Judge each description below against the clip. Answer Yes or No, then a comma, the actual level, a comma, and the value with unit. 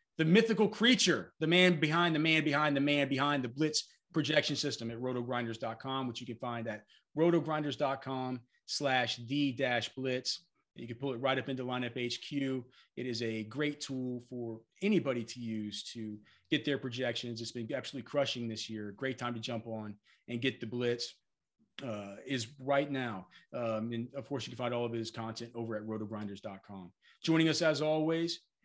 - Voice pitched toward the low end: Yes, low, 125 Hz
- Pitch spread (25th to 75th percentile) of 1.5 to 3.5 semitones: No, average, 3.9 semitones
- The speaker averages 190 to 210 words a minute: No, average, 175 wpm